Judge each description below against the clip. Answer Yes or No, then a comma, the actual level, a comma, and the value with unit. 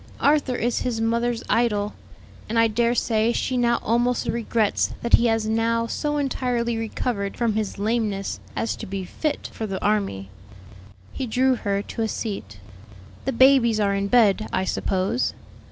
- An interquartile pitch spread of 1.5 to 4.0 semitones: Yes, narrow, 2.5 semitones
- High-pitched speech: Yes, high, 230 Hz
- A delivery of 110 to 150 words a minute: No, average, 165 wpm